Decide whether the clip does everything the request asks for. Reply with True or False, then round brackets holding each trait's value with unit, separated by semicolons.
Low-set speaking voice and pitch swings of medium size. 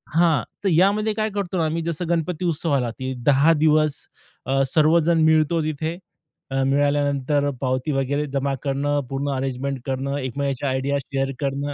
False (145 Hz; 3.0 semitones)